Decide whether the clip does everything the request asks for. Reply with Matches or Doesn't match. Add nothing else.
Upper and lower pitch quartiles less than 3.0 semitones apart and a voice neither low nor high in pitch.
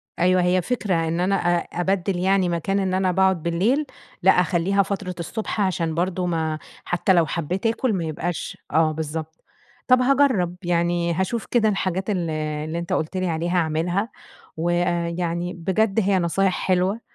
Matches